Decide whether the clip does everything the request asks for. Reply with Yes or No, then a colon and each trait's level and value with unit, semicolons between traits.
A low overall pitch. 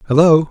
No: medium, 155 Hz